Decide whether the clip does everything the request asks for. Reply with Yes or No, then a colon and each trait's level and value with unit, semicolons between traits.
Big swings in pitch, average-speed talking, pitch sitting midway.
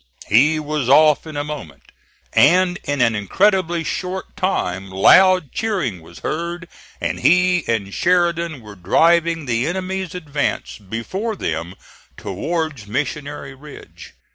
No: wide, 7.3 semitones; slow, 125 wpm; medium, 150 Hz